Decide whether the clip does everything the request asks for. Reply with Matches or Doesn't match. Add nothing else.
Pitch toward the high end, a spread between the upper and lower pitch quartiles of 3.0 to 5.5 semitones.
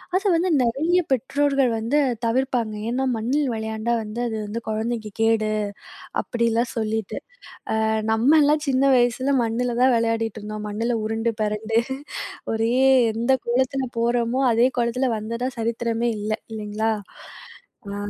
Doesn't match